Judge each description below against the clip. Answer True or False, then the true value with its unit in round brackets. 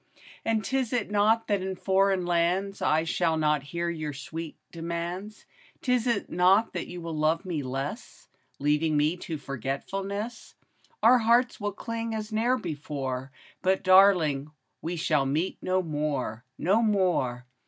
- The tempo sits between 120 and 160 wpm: True (155 wpm)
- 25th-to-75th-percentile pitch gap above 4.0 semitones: True (5.2 semitones)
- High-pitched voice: False (175 Hz)